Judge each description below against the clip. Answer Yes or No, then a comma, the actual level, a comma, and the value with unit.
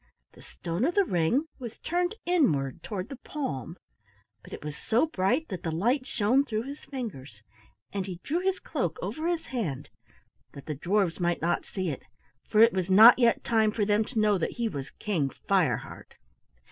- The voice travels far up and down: Yes, wide, 7.6 semitones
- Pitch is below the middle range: No, high, 215 Hz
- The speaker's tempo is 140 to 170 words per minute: No, average, 190 wpm